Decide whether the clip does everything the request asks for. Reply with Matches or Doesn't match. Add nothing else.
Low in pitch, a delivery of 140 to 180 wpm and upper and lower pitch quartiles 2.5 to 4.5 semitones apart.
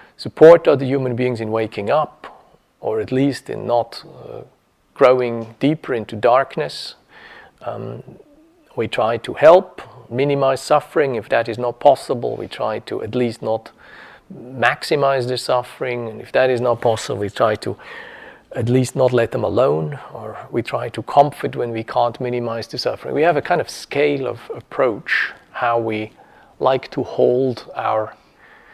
Matches